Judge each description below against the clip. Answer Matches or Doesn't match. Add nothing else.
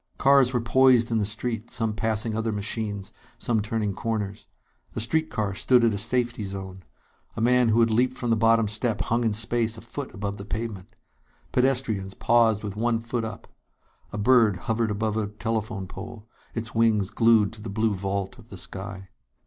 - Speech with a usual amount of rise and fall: Doesn't match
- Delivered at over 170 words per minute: Matches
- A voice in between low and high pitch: Doesn't match